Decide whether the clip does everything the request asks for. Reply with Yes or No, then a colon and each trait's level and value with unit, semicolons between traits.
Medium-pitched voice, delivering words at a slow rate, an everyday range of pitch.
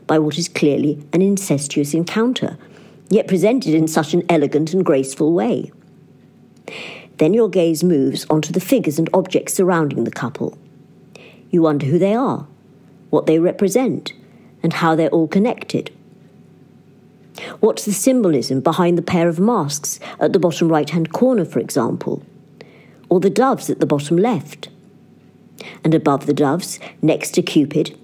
No: medium, 165 Hz; average, 150 wpm; average, 3.8 semitones